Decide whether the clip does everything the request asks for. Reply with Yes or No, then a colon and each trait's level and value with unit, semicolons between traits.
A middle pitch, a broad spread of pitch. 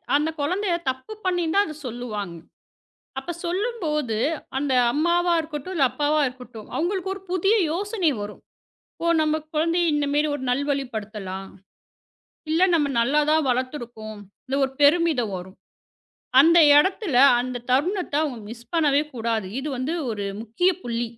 No: very high, 290 Hz; wide, 5.8 semitones